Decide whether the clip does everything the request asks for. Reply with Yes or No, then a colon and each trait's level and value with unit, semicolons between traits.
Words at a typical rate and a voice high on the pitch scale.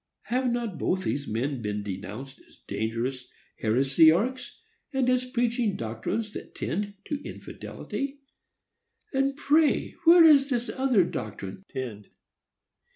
No: slow, 120 wpm; high, 200 Hz